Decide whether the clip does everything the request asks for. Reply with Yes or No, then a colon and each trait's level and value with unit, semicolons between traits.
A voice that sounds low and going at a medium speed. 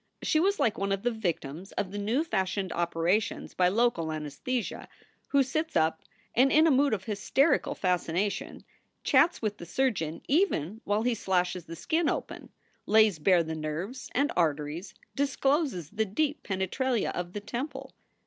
No: high, 205 Hz; average, 165 wpm